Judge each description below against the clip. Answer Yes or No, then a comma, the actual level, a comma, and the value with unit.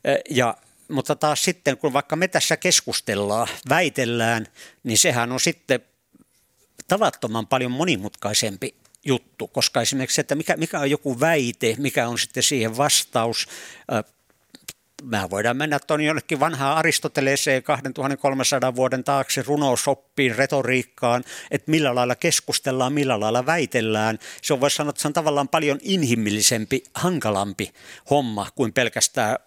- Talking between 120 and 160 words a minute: Yes, average, 130 wpm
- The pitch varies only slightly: No, average, 3.4 semitones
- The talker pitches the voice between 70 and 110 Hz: No, low, 135 Hz